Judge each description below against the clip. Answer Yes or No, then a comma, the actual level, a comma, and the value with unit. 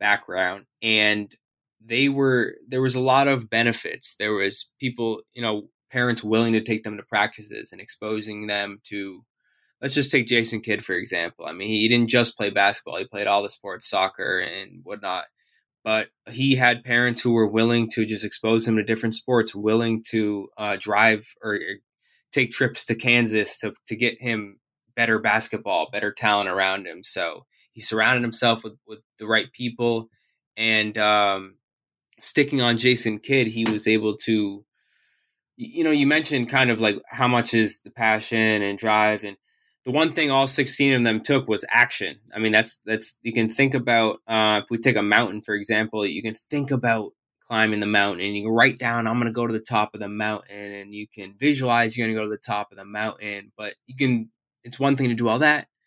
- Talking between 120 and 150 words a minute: No, average, 200 wpm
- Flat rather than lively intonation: Yes, narrow, 2.3 semitones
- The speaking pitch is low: Yes, low, 110 Hz